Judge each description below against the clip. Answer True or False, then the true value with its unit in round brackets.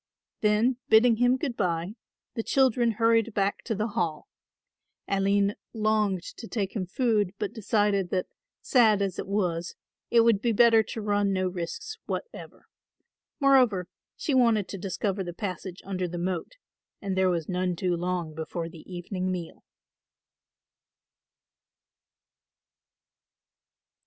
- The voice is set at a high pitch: True (200 Hz)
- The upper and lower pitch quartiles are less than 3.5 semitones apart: False (3.8 semitones)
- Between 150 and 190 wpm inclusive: False (135 wpm)